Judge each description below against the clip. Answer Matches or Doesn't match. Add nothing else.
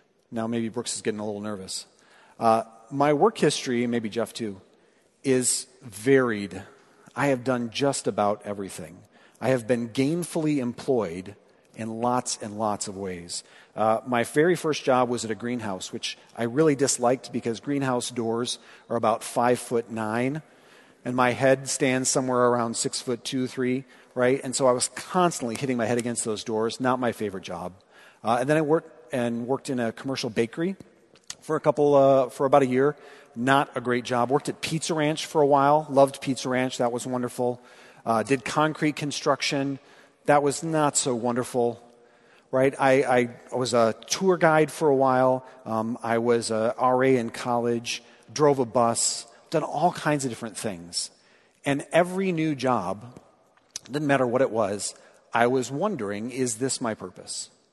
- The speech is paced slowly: Doesn't match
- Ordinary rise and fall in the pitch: Matches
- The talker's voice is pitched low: Matches